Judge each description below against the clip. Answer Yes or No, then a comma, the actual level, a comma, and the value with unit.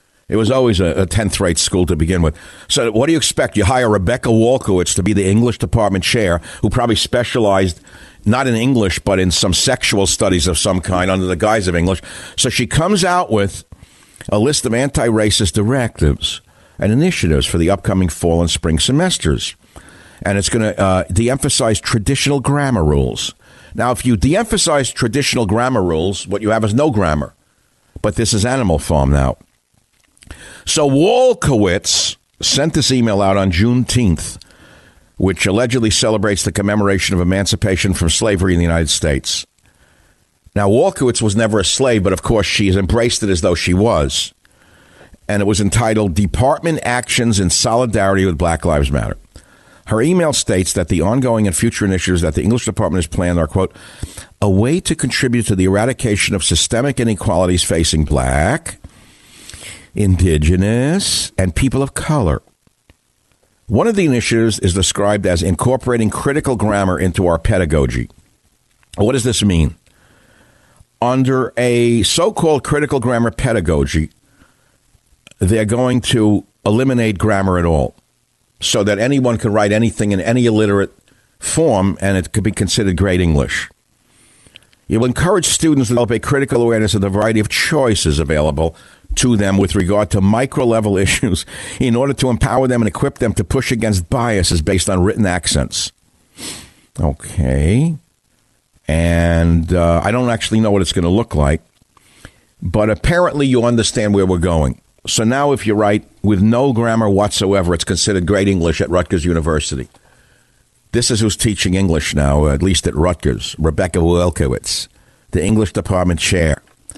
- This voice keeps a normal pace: Yes, average, 160 wpm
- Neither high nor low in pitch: No, low, 105 Hz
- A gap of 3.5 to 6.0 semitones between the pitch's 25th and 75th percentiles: Yes, average, 4.7 semitones